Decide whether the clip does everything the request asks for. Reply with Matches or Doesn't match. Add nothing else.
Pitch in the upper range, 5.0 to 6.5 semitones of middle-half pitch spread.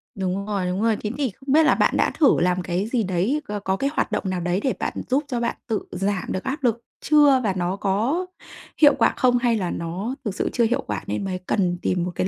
Matches